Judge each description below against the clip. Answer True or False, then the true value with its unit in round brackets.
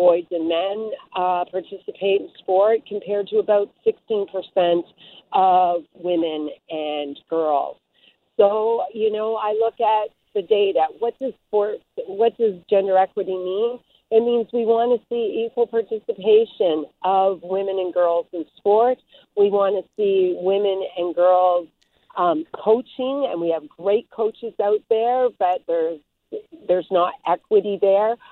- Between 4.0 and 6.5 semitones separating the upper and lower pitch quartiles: True (4.5 semitones)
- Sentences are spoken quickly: False (140 wpm)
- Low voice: False (205 Hz)